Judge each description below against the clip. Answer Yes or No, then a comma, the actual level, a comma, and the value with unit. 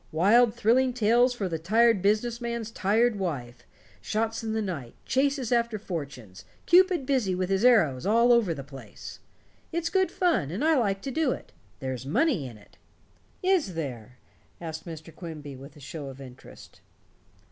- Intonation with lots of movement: Yes, wide, 7.9 semitones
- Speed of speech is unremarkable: Yes, average, 170 wpm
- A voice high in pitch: Yes, high, 205 Hz